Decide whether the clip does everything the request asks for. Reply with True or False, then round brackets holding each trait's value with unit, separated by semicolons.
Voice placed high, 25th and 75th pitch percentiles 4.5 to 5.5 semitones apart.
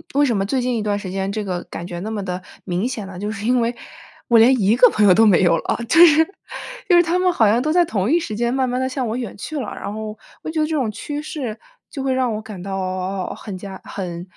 True (220 Hz; 5.1 semitones)